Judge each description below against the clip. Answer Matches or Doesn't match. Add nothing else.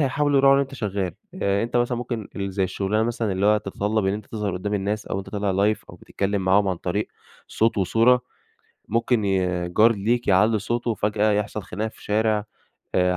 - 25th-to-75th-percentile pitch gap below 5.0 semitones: Matches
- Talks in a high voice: Doesn't match